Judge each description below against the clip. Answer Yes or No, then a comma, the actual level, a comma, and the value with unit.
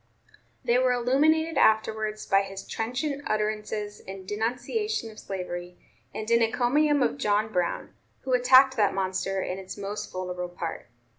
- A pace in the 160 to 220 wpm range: No, average, 145 wpm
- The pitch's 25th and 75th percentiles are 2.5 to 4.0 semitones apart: No, average, 4.5 semitones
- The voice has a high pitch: Yes, high, 215 Hz